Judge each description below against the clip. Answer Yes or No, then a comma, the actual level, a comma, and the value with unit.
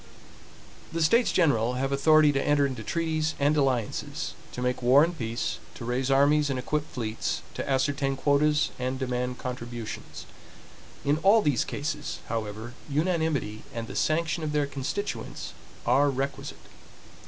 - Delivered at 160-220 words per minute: No, average, 145 wpm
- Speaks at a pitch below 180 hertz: Yes, medium, 140 Hz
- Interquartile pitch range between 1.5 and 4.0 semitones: Yes, average, 3.4 semitones